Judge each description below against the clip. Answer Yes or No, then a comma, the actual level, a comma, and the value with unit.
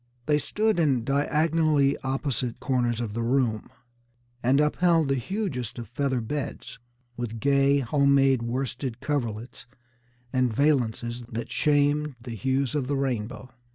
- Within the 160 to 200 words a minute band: No, slow, 135 wpm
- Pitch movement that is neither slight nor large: Yes, average, 3.3 semitones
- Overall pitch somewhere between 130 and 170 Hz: Yes, low, 135 Hz